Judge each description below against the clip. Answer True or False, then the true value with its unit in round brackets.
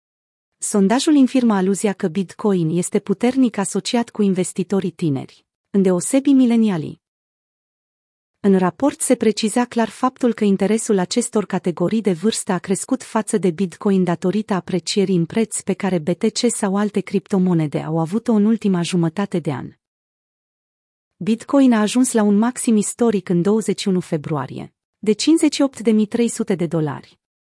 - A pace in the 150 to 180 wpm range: False (135 wpm)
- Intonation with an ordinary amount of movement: True (3.7 semitones)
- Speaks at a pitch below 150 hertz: False (205 Hz)